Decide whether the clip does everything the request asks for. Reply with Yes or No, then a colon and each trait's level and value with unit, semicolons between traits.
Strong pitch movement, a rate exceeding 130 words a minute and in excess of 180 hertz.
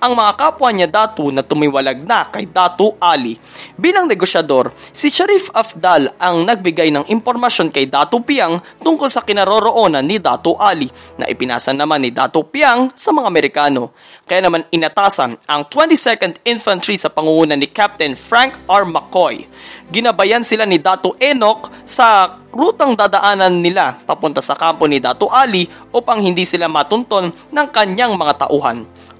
Yes: wide, 7.5 semitones; average, 150 wpm; high, 190 Hz